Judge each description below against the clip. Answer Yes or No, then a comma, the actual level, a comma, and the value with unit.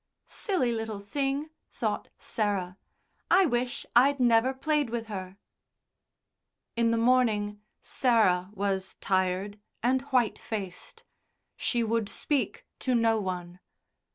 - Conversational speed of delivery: No, slow, 115 wpm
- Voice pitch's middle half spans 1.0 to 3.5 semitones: No, average, 4.1 semitones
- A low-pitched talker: No, high, 225 Hz